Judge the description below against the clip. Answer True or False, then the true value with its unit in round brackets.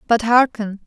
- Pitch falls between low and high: False (225 Hz)